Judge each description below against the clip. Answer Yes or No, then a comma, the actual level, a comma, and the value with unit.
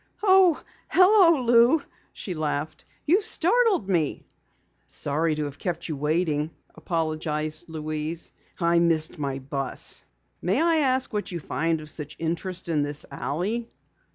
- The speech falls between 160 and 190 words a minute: No, slow, 135 wpm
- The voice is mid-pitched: Yes, medium, 165 Hz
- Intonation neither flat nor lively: No, wide, 7.6 semitones